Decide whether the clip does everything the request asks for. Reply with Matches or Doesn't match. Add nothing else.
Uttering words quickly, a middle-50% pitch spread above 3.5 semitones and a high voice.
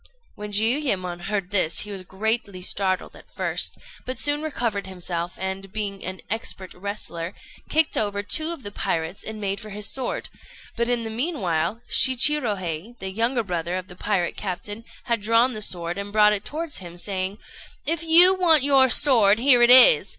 Doesn't match